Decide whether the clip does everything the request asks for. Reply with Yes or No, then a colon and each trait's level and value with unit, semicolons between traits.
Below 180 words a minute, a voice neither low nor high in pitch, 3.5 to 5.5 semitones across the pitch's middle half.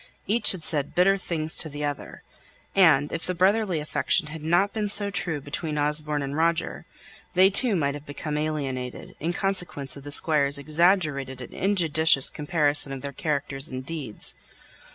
Yes: average, 170 wpm; medium, 155 Hz; average, 3.8 semitones